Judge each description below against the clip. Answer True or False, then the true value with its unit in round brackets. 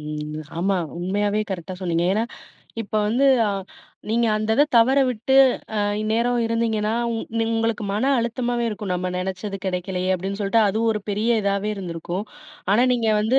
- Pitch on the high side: True (210 Hz)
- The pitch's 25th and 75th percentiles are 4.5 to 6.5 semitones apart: False (3.5 semitones)